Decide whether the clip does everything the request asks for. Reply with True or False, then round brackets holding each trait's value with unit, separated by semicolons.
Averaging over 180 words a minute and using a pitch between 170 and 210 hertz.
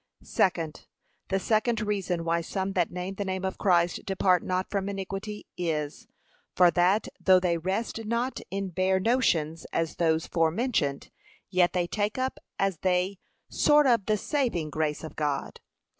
False (160 wpm; 185 Hz)